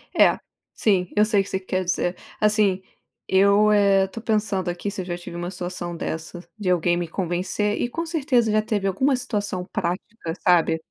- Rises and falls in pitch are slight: No, average, 3.1 semitones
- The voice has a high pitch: Yes, high, 195 Hz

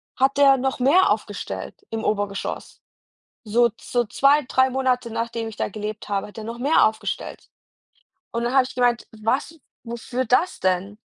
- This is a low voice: No, high, 240 Hz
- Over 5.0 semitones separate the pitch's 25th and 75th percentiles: No, average, 3.3 semitones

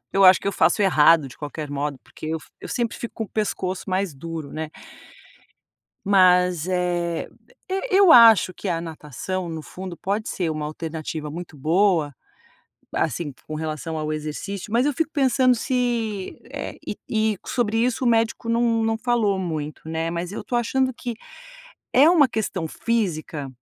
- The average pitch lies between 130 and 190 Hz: Yes, medium, 185 Hz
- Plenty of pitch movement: Yes, wide, 6.3 semitones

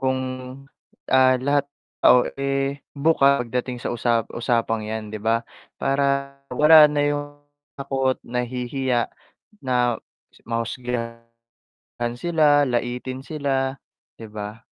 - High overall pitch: No, low, 130 Hz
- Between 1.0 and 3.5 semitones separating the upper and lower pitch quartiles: Yes, average, 2.8 semitones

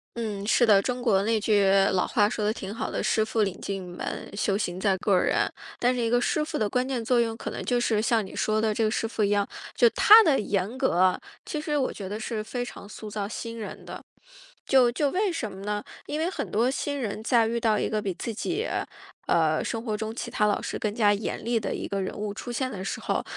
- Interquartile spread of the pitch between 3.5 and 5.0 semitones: No, average, 3.0 semitones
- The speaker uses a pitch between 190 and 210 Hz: No, high, 220 Hz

